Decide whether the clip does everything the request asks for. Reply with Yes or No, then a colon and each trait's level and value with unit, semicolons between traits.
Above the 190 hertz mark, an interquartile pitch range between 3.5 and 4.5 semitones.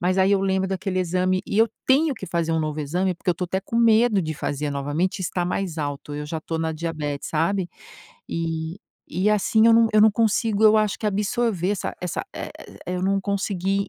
No: medium, 185 Hz; average, 4.0 semitones